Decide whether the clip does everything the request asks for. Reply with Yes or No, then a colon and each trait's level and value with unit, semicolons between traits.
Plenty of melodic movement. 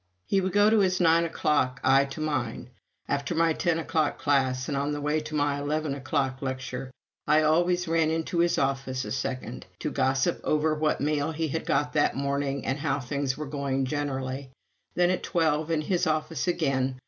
No: average, 3.0 semitones